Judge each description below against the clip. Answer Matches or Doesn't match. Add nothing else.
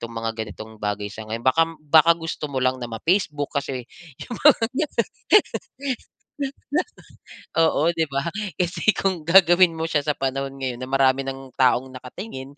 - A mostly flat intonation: Doesn't match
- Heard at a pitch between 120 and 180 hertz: Matches